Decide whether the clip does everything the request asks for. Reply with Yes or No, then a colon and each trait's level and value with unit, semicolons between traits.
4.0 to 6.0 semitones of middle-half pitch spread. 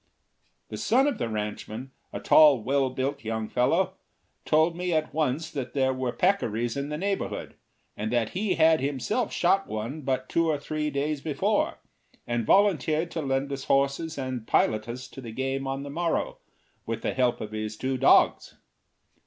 Yes: average, 4.4 semitones